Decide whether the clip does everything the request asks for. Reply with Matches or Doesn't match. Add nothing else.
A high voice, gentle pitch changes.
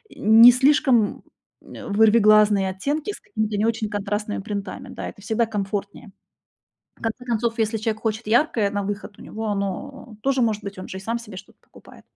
Matches